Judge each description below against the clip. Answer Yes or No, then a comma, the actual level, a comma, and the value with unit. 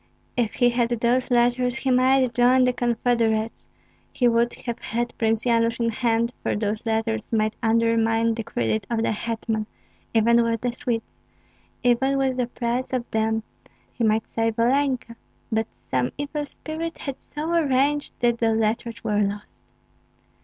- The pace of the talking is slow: No, average, 160 wpm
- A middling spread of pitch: No, narrow, 1.9 semitones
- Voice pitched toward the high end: Yes, high, 235 Hz